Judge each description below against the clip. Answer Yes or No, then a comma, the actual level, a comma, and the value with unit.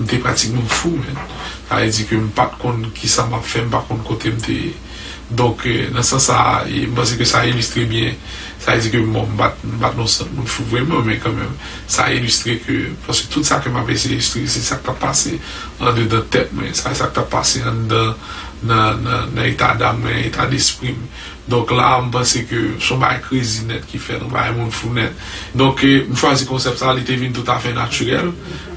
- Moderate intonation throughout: No, narrow, 1.8 semitones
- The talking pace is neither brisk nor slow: No, fast, 250 wpm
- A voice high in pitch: No, low, 120 Hz